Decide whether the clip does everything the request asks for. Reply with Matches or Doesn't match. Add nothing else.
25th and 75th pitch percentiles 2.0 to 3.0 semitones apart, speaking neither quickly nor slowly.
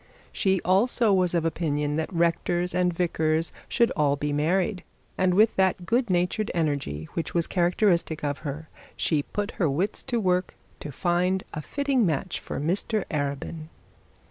Doesn't match